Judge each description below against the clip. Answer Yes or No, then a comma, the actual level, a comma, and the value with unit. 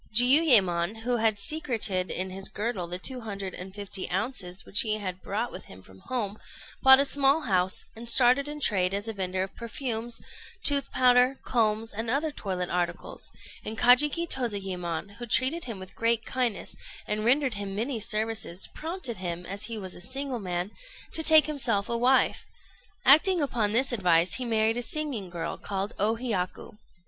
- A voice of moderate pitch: No, high, 220 Hz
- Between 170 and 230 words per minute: Yes, average, 180 wpm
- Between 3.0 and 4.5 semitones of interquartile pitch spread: No, average, 5.0 semitones